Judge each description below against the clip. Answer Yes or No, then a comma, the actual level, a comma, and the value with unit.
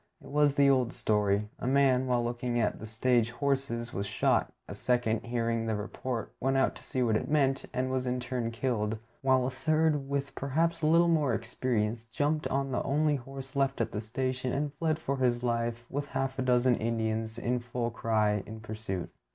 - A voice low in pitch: Yes, low, 125 Hz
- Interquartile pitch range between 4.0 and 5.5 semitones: No, average, 3.0 semitones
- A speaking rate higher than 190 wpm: Yes, average, 200 wpm